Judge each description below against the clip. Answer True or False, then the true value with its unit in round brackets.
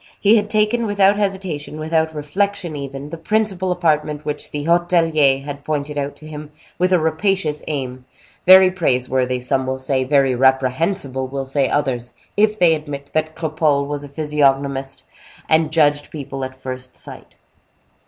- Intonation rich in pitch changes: False (4.1 semitones)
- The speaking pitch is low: False (150 Hz)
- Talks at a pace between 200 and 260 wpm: False (155 wpm)